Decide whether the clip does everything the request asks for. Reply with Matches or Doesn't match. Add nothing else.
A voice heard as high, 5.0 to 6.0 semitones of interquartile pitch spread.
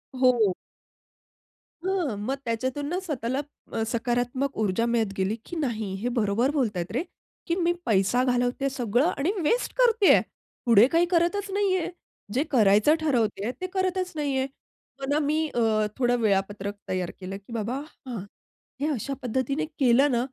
Matches